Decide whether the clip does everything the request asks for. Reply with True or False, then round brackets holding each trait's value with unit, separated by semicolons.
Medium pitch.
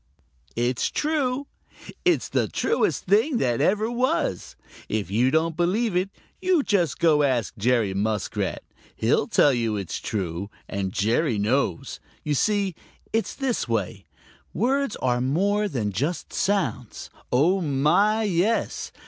True (150 Hz)